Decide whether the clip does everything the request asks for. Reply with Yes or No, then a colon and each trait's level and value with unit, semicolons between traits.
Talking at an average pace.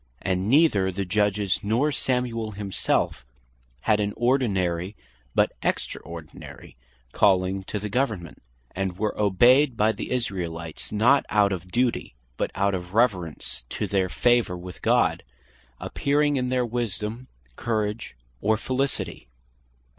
No: slow, 125 wpm